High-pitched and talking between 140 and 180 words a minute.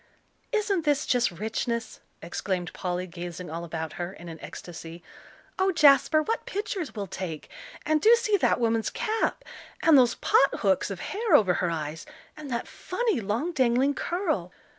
Yes: high, 235 Hz; average, 160 wpm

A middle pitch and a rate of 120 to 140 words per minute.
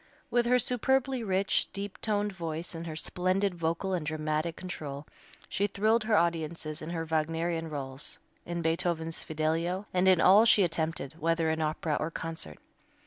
No: medium, 170 Hz; average, 160 wpm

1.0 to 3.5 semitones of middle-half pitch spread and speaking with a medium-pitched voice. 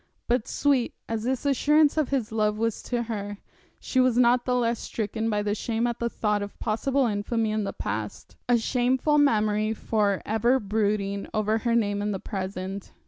No: average, 2.8 semitones; high, 225 Hz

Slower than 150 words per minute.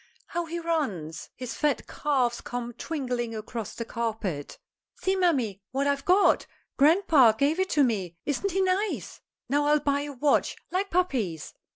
No: average, 160 wpm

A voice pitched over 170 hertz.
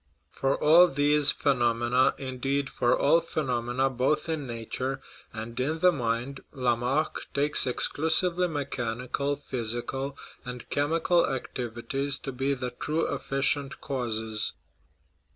No: low, 135 Hz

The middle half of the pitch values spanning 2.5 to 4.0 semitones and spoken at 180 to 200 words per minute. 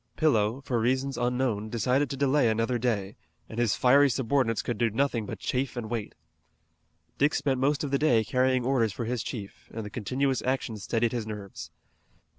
Yes: average, 3.1 semitones; average, 185 wpm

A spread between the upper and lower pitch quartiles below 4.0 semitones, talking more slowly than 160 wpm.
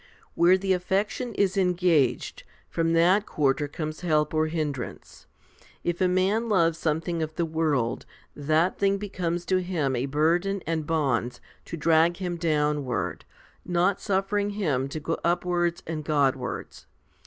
Yes: average, 3.3 semitones; average, 150 wpm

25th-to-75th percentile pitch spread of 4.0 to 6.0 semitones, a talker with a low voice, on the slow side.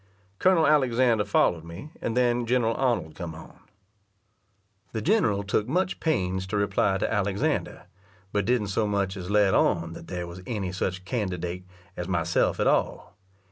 No: average, 4.8 semitones; low, 100 Hz; average, 160 wpm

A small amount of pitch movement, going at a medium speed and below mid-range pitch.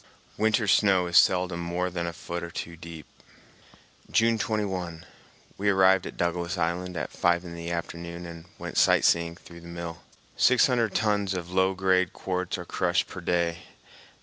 Yes: narrow, 1.8 semitones; average, 175 wpm; very low, 90 Hz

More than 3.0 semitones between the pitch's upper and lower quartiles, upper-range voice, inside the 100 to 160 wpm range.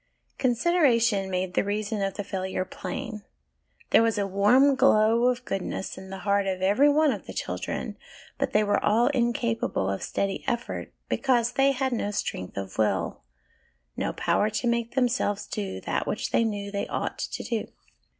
No: average, 3.7 semitones; high, 215 Hz; average, 175 wpm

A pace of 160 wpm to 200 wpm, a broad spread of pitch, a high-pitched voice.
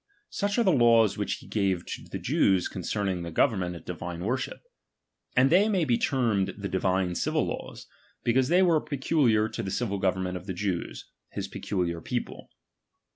No: average, 180 wpm; wide, 6.2 semitones; low, 105 Hz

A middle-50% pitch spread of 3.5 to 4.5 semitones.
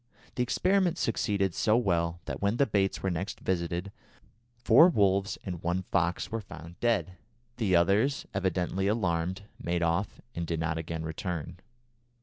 Yes: average, 3.8 semitones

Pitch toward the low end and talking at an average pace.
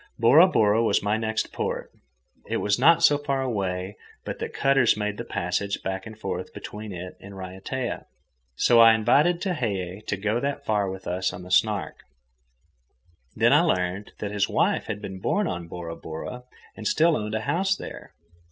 Yes: low, 105 Hz; average, 180 wpm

